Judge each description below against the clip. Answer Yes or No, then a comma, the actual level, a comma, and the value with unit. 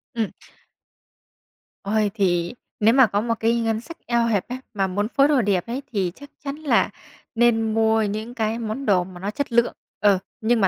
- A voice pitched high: Yes, high, 225 Hz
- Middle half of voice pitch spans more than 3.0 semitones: No, average, 2.7 semitones